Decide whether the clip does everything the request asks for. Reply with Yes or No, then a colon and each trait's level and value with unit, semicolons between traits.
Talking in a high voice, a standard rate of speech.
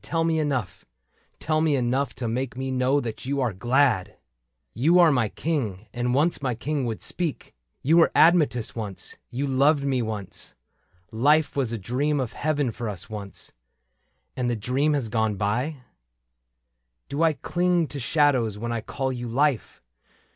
No: low, 130 Hz; average, 180 wpm